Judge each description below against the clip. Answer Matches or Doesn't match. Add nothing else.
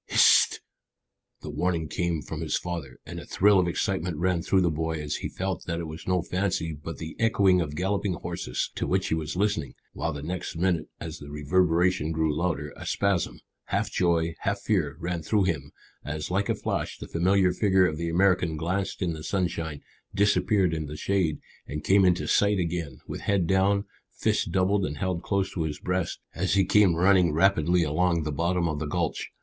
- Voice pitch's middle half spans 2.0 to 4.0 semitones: Matches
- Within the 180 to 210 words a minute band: Matches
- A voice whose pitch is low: Matches